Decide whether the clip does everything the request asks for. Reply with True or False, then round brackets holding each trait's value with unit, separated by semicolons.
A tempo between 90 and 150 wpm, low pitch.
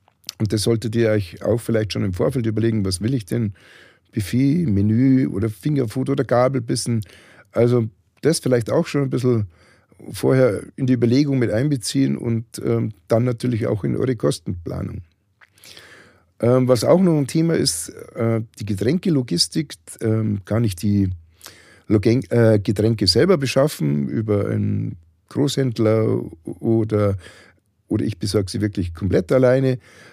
True (145 wpm; 115 Hz)